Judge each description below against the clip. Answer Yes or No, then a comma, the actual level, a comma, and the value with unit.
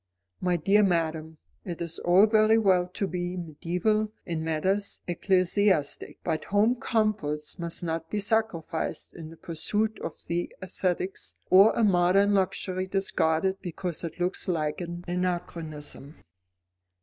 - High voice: No, medium, 180 Hz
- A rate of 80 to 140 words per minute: Yes, slow, 135 wpm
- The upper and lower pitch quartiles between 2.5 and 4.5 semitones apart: Yes, average, 3.2 semitones